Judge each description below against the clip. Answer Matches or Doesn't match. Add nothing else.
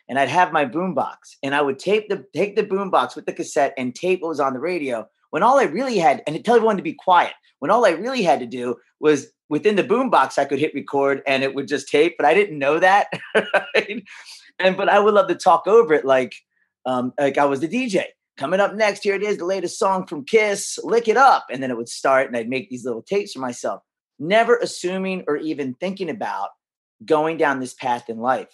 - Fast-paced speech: Matches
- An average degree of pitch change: Doesn't match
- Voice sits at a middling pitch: Matches